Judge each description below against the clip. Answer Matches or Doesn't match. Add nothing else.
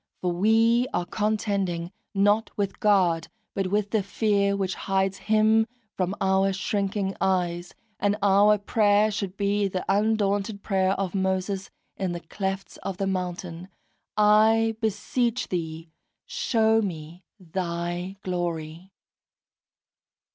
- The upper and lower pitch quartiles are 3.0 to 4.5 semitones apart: Doesn't match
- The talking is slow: Matches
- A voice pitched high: Matches